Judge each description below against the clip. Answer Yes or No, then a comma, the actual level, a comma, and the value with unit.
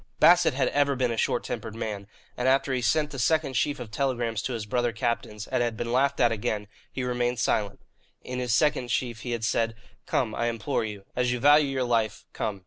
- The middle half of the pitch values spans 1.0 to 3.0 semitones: Yes, average, 2.7 semitones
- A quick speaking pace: Yes, fast, 225 wpm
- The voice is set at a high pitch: No, low, 120 Hz